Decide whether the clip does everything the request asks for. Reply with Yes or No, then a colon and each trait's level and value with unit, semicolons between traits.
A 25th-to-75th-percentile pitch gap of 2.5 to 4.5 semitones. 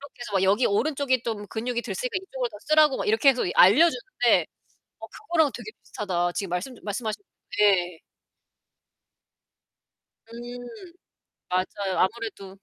No: average, 5.3 semitones